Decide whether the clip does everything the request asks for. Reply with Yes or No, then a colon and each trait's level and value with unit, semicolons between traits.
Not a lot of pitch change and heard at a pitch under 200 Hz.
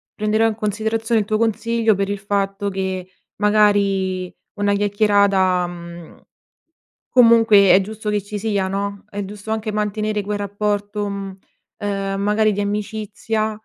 No: narrow, 1.4 semitones; high, 205 Hz